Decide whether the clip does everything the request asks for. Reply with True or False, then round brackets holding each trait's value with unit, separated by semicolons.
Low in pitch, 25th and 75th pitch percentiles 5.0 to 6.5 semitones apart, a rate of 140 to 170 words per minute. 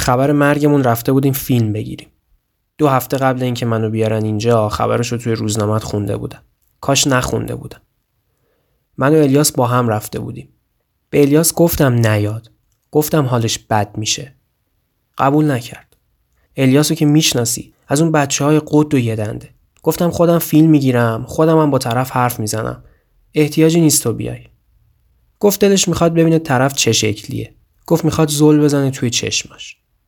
True (130 Hz; 5.3 semitones; 150 wpm)